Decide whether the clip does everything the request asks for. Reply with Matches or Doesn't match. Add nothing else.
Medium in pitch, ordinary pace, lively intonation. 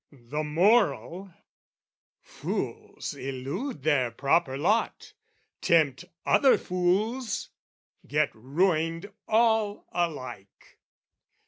Doesn't match